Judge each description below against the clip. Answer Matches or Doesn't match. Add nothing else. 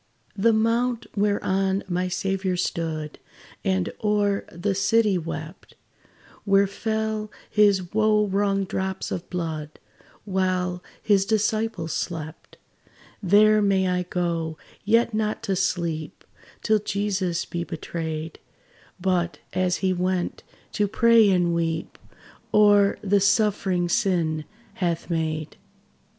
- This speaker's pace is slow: Matches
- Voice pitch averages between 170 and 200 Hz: Matches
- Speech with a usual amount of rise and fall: Matches